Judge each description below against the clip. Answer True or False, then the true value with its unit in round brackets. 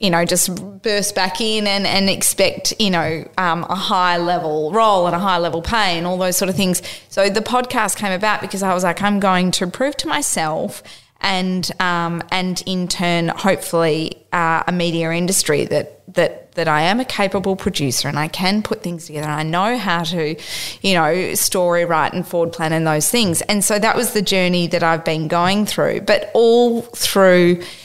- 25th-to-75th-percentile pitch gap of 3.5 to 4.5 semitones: False (2.8 semitones)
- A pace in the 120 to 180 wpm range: False (205 wpm)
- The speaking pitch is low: False (180 Hz)